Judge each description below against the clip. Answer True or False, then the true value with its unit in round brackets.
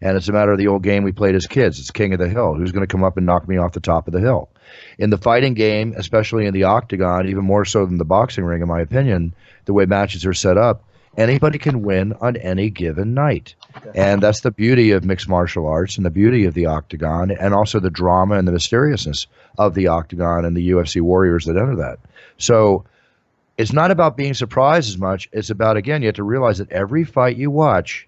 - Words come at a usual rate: False (240 wpm)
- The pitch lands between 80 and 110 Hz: True (100 Hz)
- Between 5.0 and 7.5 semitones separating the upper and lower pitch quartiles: False (3.8 semitones)